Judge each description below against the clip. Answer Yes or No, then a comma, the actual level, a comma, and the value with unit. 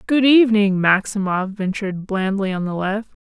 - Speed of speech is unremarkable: Yes, average, 150 wpm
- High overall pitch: Yes, high, 205 Hz